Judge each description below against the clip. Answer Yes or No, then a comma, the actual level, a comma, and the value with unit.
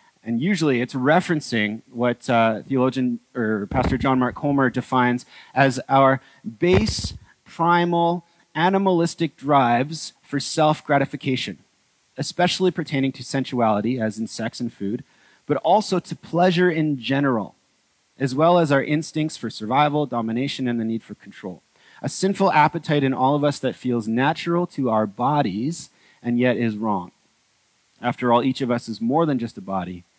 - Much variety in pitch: No, average, 4.8 semitones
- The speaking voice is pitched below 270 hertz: Yes, low, 135 Hz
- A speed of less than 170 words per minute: Yes, average, 155 wpm